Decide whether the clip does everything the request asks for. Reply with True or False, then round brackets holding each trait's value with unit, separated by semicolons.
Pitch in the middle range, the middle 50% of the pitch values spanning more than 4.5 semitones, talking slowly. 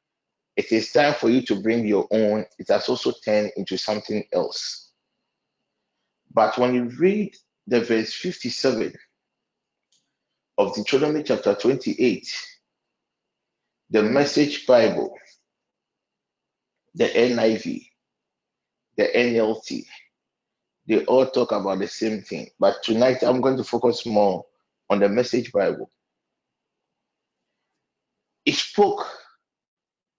False (120 Hz; 5.1 semitones; 110 wpm)